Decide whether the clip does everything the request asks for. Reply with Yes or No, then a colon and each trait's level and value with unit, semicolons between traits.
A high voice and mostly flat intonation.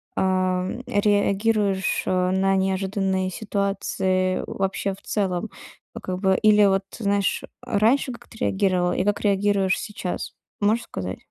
Yes: high, 195 Hz; narrow, 1.6 semitones